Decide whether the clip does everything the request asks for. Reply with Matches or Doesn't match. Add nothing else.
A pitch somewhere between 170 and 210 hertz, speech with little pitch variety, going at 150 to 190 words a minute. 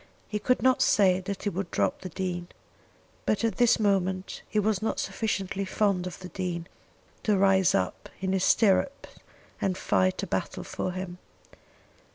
Matches